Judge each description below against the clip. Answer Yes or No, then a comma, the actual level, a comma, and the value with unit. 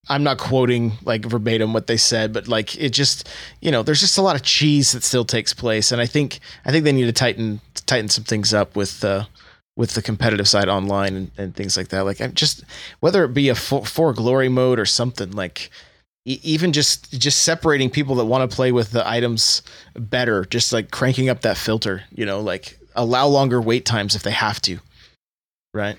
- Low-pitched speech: Yes, low, 120 Hz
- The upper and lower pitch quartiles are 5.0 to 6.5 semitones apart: No, average, 3.5 semitones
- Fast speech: Yes, fast, 220 wpm